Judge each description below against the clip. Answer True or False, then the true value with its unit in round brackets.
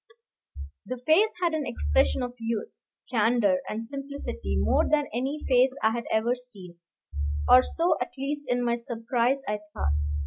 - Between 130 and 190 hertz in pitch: False (245 Hz)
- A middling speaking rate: True (160 wpm)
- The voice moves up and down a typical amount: True (3.8 semitones)